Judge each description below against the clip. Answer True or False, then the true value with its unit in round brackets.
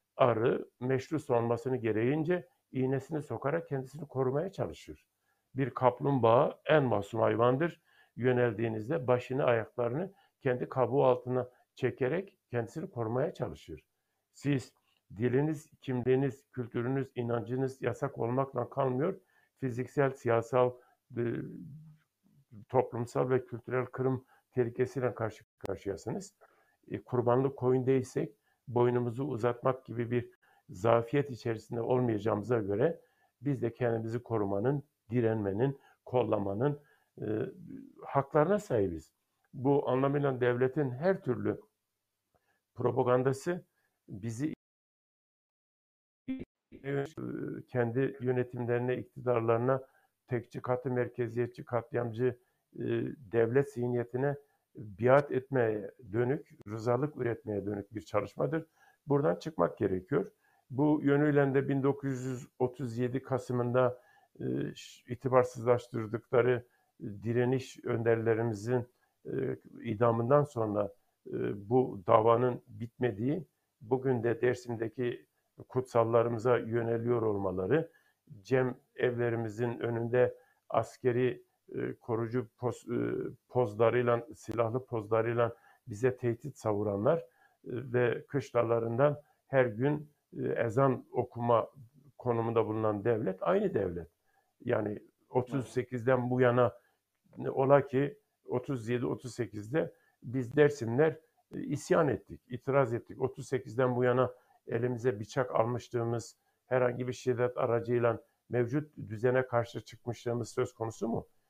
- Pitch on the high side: False (125 Hz)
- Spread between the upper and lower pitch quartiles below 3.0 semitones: True (2.5 semitones)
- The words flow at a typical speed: False (85 wpm)